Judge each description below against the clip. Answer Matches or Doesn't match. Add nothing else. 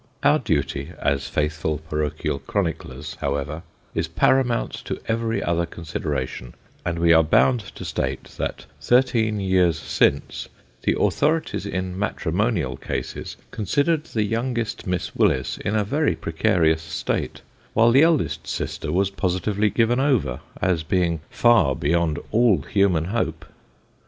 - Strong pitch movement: Matches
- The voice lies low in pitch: Matches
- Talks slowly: Matches